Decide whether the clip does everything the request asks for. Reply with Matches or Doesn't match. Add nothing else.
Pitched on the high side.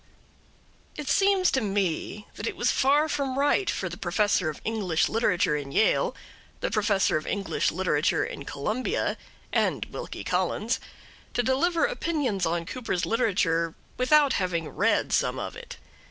Matches